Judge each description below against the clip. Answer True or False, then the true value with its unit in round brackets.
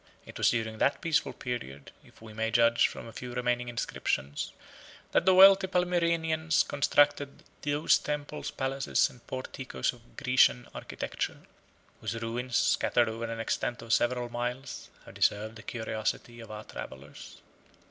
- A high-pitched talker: False (120 Hz)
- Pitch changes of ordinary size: True (4.2 semitones)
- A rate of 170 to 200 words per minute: False (145 wpm)